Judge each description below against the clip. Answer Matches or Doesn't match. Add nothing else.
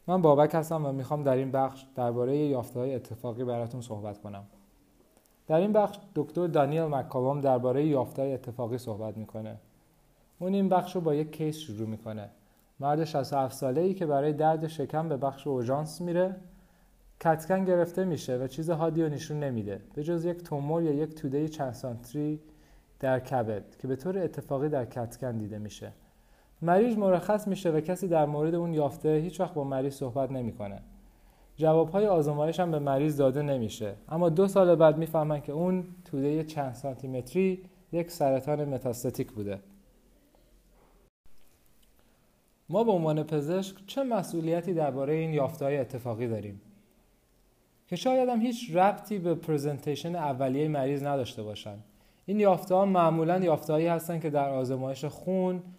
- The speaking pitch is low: Doesn't match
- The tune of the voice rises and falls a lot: Doesn't match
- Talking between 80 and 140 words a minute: Doesn't match